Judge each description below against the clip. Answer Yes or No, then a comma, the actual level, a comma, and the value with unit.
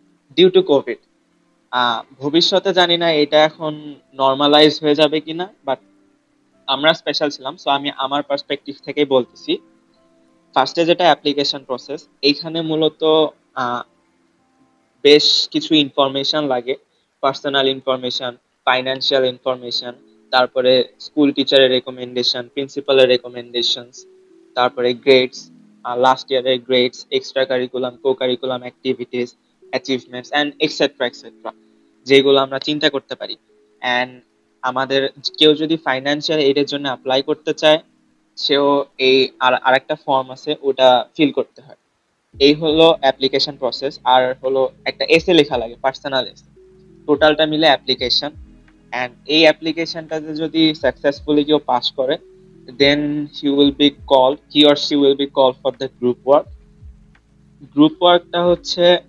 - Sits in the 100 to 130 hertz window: No, medium, 140 Hz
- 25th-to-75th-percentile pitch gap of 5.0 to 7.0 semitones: No, average, 3.1 semitones